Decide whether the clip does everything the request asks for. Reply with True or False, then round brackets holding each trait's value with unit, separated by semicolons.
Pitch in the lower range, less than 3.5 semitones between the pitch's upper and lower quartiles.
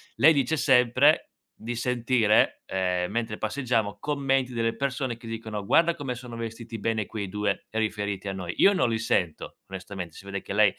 False (115 Hz; 3.8 semitones)